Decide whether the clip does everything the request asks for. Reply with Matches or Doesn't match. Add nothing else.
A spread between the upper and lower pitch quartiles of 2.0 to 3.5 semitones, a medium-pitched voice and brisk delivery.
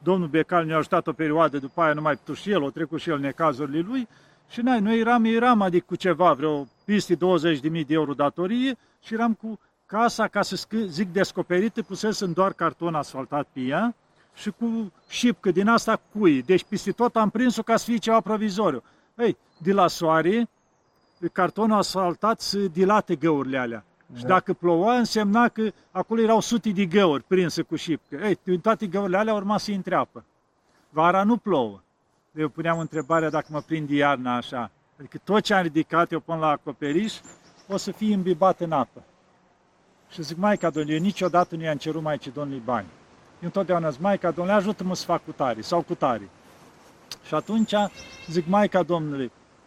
Doesn't match